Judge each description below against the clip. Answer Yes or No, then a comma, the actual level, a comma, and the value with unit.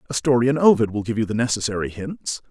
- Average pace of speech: No, fast, 240 wpm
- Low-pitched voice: Yes, low, 115 Hz